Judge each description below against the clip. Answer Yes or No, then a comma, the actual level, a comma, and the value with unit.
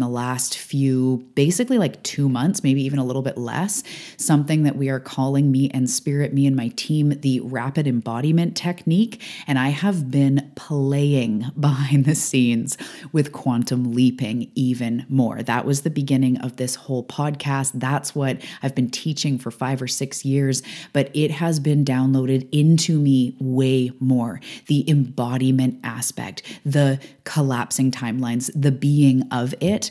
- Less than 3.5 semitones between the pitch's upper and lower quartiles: Yes, narrow, 2.4 semitones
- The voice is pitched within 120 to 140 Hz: Yes, low, 135 Hz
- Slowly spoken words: No, average, 160 wpm